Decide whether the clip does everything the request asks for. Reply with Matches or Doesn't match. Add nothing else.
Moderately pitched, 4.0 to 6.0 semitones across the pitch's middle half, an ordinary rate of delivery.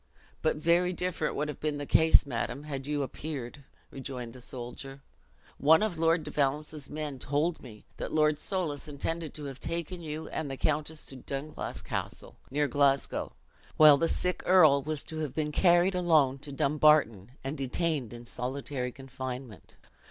Doesn't match